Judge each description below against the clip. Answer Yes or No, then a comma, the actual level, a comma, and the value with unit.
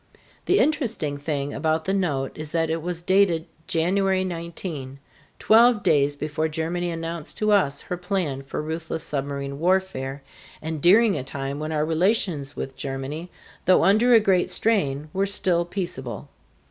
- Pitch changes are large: No, average, 4.7 semitones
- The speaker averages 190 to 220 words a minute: No, average, 155 wpm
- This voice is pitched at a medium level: Yes, medium, 165 Hz